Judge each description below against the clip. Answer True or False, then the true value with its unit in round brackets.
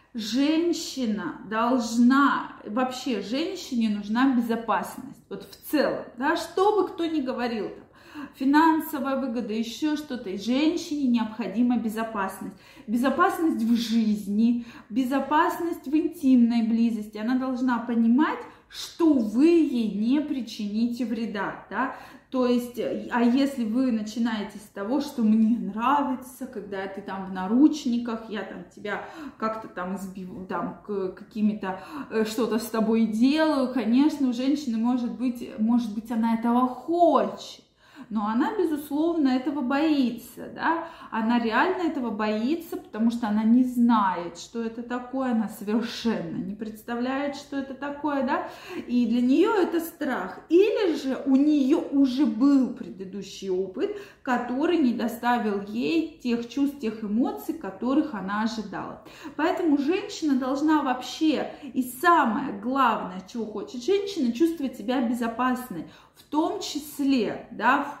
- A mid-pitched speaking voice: False (250 Hz)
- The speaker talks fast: False (130 wpm)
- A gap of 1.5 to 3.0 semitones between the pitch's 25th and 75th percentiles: False (4.5 semitones)